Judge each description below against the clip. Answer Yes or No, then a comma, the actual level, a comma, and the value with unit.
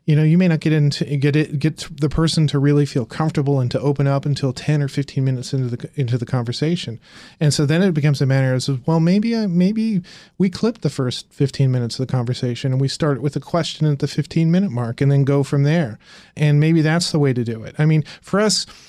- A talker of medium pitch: Yes, medium, 150 Hz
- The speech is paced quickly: Yes, fast, 250 wpm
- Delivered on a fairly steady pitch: No, average, 3.0 semitones